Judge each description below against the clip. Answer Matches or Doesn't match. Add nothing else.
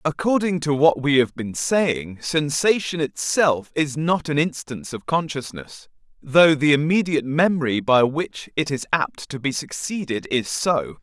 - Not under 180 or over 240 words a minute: Doesn't match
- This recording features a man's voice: Matches